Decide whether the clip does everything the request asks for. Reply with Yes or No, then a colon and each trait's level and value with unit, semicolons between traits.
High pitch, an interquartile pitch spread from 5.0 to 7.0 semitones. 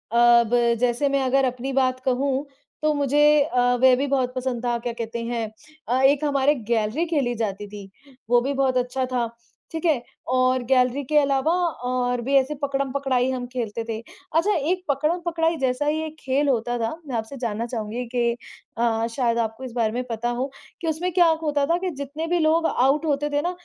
No: very high, 260 Hz; average, 3.3 semitones